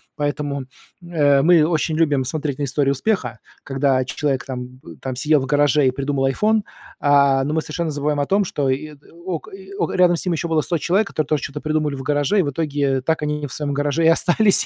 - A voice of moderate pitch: Yes, medium, 145 Hz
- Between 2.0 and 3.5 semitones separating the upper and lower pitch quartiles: Yes, average, 2.8 semitones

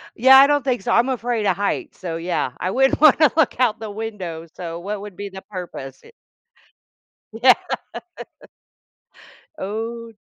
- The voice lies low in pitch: No, high, 210 Hz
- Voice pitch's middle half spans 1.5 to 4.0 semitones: No, average, 5.2 semitones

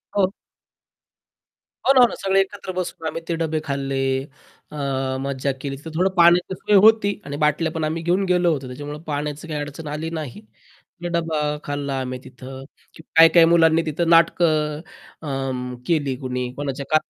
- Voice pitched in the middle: Yes, medium, 155 Hz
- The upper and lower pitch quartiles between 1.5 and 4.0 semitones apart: Yes, average, 3.3 semitones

